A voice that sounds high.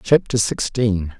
No: low, 110 Hz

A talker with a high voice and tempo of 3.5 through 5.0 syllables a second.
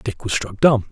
No: low, 110 Hz; 4.8 syllables/s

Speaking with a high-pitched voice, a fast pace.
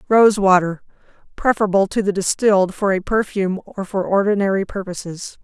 No: high, 195 Hz; slow, 135 wpm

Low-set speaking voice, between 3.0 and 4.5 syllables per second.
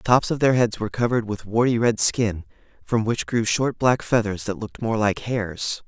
No: low, 115 Hz; 5.2 syllables/s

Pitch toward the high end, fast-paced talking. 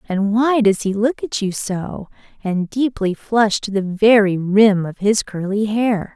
No: high, 210 Hz; average, 185 wpm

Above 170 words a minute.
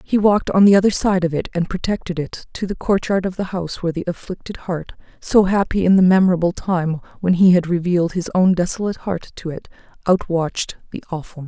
Yes: fast, 205 wpm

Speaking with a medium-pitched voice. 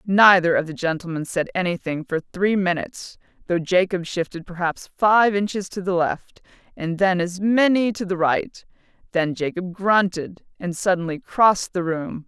Yes: medium, 180 Hz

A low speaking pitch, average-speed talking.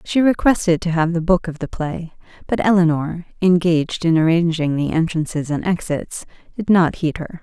No: medium, 170 Hz; average, 180 wpm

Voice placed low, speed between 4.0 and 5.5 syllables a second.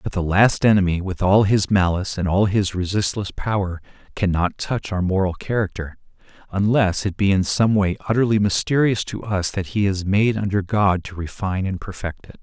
Yes: low, 100 Hz; 5.2 syllables/s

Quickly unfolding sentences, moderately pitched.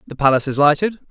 Yes: fast, 220 wpm; medium, 150 Hz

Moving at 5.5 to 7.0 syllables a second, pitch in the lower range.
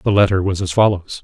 Yes: 5.9 syllables/s; very low, 95 Hz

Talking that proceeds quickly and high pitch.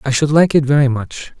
No: fast, 255 wpm; medium, 140 Hz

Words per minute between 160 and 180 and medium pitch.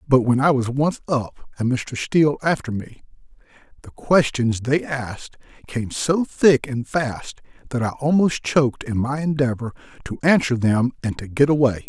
No: average, 170 wpm; low, 130 Hz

